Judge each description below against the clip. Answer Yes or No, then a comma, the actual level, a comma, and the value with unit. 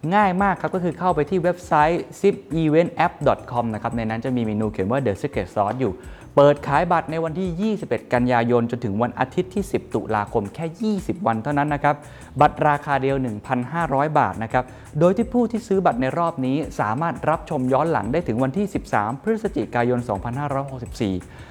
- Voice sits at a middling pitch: Yes, medium, 145 Hz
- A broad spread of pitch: Yes, wide, 5.9 semitones